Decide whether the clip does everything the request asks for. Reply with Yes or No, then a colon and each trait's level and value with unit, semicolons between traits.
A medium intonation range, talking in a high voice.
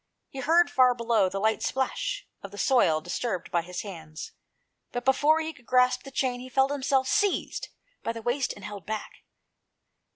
Yes: average, 4.7 semitones; high, 245 Hz